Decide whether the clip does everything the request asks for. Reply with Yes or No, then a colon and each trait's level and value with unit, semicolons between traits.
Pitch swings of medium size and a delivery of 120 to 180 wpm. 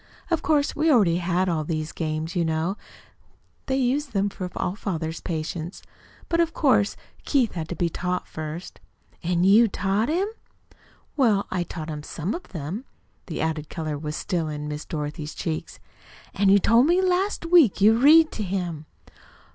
No: wide, 7.0 semitones; average, 170 wpm